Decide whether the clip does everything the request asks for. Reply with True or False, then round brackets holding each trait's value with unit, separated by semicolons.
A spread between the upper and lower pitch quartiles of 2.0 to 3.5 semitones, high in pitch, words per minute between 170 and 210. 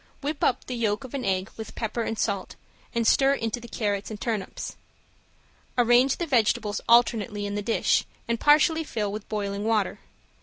True (2.9 semitones; 225 Hz; 180 wpm)